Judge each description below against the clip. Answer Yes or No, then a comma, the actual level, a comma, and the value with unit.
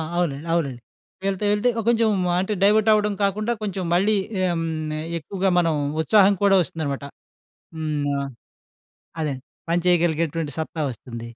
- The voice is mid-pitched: Yes, medium, 175 Hz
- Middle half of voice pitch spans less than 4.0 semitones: No, average, 4.7 semitones